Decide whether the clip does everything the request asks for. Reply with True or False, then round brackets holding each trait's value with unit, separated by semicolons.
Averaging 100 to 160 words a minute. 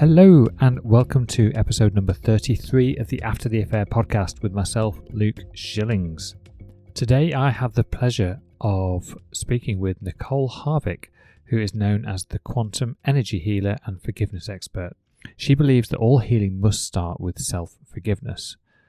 True (155 wpm)